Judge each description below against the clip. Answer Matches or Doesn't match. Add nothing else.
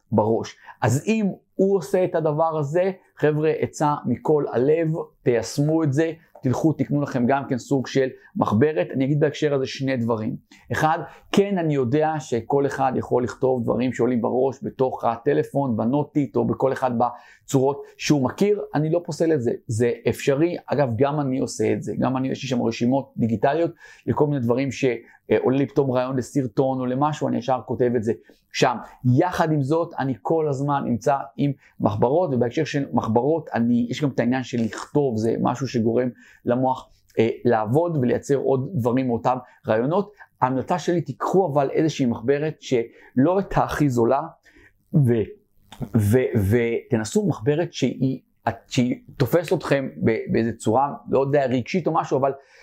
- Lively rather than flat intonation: Doesn't match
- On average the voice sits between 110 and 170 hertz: Matches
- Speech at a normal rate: Doesn't match